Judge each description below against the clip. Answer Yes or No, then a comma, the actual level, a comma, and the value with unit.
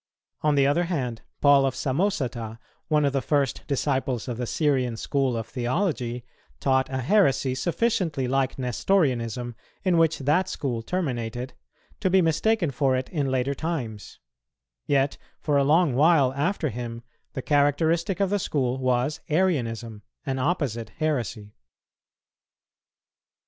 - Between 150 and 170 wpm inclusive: No, average, 140 wpm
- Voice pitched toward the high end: No, low, 135 Hz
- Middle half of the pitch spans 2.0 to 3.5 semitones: No, average, 4.2 semitones